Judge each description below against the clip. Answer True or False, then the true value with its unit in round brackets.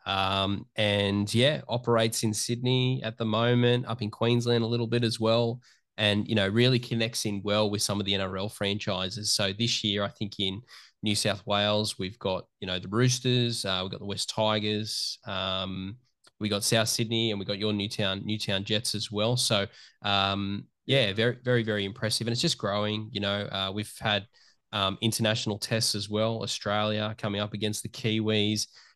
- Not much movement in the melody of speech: True (2.2 semitones)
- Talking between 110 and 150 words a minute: False (190 wpm)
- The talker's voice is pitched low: True (105 Hz)